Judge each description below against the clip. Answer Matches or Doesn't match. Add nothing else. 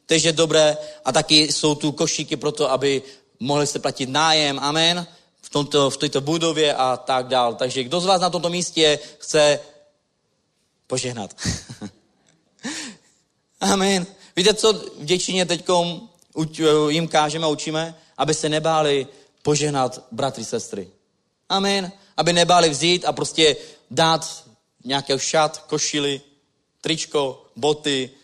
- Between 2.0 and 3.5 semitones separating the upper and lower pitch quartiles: Matches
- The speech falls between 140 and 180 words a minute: Doesn't match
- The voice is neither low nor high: Matches